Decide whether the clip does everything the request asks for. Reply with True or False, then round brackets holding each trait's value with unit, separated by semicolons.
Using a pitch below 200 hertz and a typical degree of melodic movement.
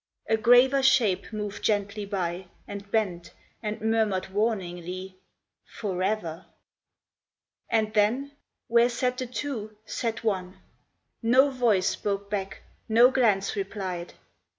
False (210 Hz; 3.4 semitones)